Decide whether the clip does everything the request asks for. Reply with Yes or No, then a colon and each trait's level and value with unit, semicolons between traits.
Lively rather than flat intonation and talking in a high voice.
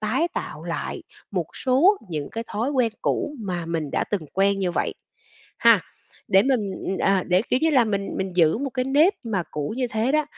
Yes: wide, 6.0 semitones; high, 215 Hz